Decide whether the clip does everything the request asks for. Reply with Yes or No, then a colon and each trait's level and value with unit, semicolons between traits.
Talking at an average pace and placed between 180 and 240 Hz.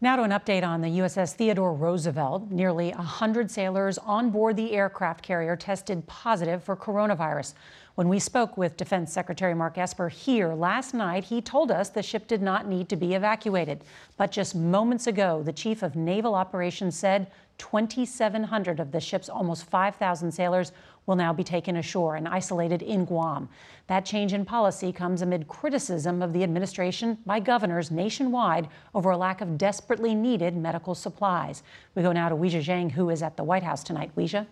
Yes: average, 180 wpm; medium, 185 Hz